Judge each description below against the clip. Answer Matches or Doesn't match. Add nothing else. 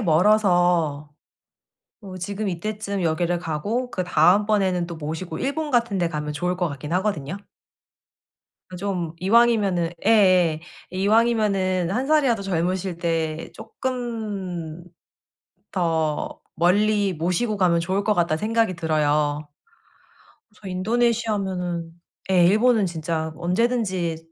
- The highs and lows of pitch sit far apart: Doesn't match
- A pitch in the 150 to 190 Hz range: Matches